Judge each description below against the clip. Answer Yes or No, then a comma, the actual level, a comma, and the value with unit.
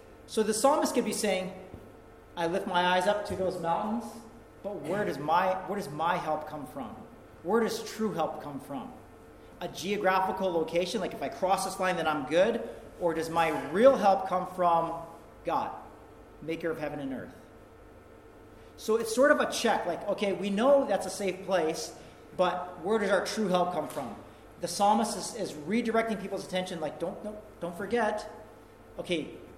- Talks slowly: No, average, 185 wpm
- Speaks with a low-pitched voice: No, high, 190 Hz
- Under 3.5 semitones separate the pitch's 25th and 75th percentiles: No, average, 4.2 semitones